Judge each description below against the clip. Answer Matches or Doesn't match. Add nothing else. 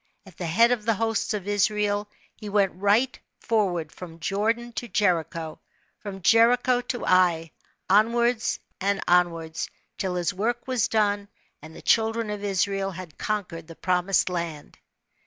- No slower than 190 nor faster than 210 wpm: Doesn't match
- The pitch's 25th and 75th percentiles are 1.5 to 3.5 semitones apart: Doesn't match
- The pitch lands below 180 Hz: Doesn't match